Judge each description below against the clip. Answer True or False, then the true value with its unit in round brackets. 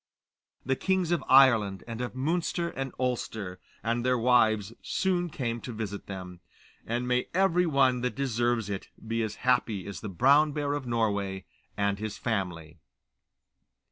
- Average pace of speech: True (155 wpm)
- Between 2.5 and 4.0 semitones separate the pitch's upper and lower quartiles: False (4.7 semitones)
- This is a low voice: True (120 Hz)